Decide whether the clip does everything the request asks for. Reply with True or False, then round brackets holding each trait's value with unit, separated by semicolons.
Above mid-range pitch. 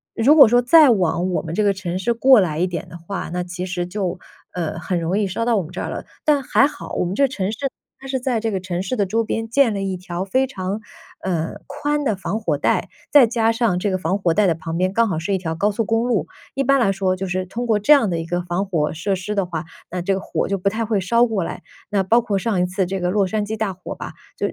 True (195 Hz)